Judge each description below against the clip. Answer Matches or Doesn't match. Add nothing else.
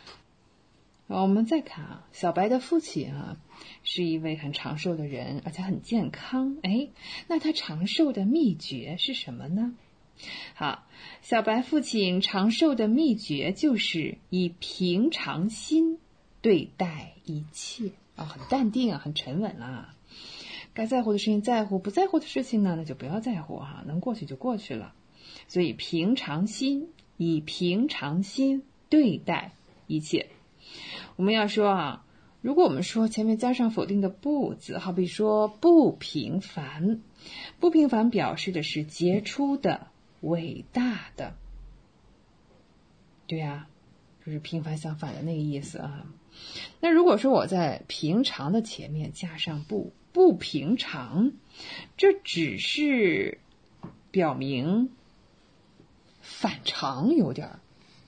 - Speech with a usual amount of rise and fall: Doesn't match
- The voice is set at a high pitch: Matches